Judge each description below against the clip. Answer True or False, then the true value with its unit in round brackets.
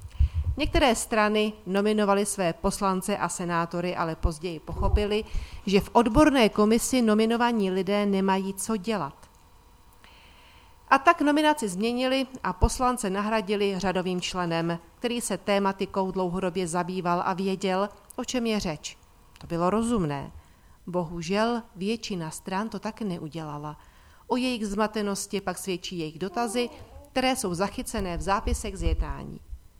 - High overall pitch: True (195 Hz)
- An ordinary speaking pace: True (125 wpm)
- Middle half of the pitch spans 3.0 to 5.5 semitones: True (4.0 semitones)